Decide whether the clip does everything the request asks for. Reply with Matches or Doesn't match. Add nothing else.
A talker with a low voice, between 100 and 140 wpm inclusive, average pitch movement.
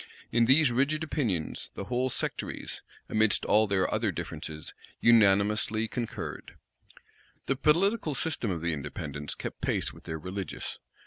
Doesn't match